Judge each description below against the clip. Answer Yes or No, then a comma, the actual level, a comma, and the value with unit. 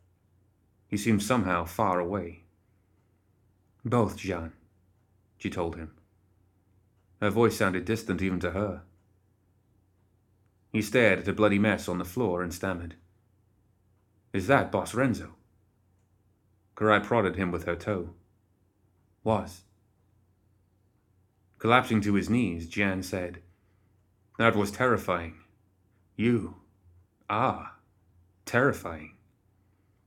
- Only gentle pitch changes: Yes, narrow, 2.1 semitones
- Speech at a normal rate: No, slow, 100 wpm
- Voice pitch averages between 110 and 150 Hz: No, very low, 95 Hz